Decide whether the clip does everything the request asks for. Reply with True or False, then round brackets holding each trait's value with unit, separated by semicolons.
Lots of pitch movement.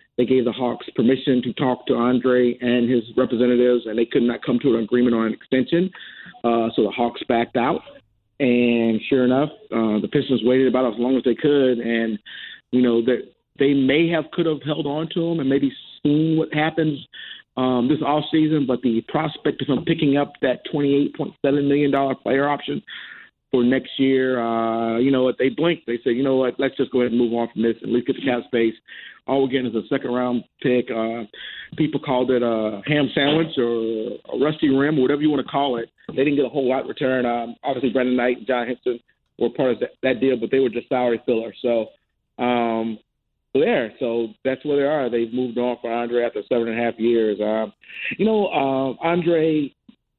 False (2.9 semitones)